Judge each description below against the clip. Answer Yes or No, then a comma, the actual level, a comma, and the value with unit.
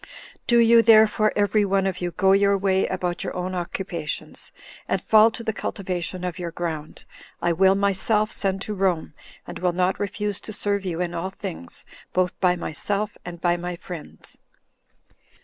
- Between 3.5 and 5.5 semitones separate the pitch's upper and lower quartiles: No, narrow, 2.5 semitones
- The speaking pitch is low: No, high, 190 Hz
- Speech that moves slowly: No, average, 175 wpm